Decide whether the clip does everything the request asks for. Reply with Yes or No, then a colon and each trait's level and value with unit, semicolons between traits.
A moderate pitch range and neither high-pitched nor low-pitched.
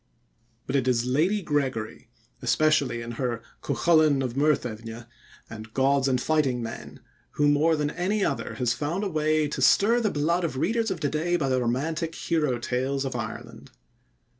Yes: average, 4.3 semitones; medium, 145 Hz